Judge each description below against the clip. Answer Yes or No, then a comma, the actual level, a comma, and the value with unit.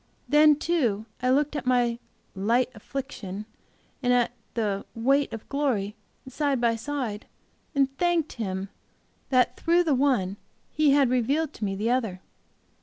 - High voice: Yes, very high, 250 Hz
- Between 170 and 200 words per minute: No, average, 145 wpm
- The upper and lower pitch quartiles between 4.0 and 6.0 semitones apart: Yes, average, 4.6 semitones